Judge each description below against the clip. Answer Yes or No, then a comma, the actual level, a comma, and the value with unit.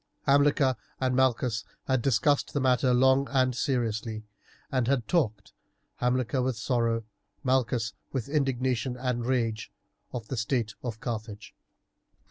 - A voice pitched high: No, low, 125 Hz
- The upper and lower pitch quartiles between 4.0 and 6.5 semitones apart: No, narrow, 2.4 semitones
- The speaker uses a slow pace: Yes, slow, 125 wpm